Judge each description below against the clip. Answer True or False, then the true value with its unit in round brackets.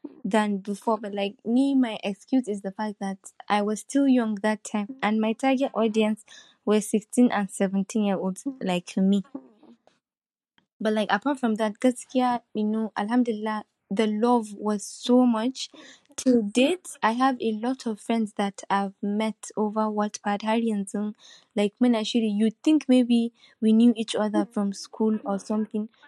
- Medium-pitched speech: False (220 Hz)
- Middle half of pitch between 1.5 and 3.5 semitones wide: True (2.9 semitones)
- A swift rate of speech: False (170 wpm)